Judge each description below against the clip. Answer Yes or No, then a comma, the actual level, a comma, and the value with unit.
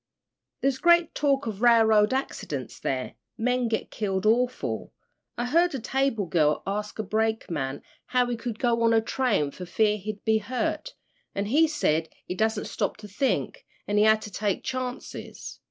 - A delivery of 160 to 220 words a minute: Yes, average, 170 wpm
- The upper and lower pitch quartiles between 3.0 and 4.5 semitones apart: Yes, average, 3.5 semitones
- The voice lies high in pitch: Yes, high, 220 Hz